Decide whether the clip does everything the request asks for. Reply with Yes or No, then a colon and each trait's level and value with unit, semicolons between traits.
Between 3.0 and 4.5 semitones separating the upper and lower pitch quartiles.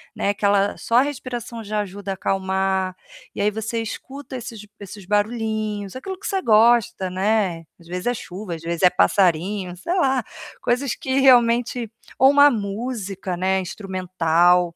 Yes: average, 4.2 semitones